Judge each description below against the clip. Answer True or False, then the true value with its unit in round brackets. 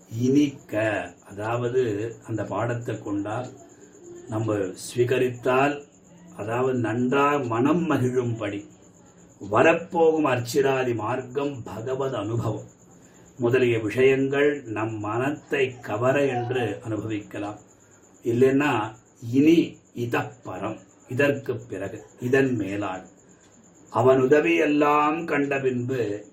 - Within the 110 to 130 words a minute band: False (80 wpm)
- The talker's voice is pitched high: False (125 Hz)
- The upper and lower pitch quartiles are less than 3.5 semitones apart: False (4.6 semitones)